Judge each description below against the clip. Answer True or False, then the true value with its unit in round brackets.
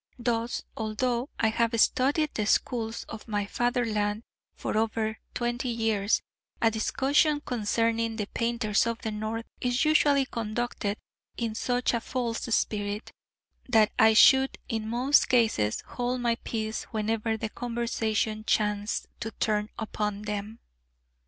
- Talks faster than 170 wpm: False (135 wpm)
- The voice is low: False (225 Hz)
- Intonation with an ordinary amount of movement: False (2.0 semitones)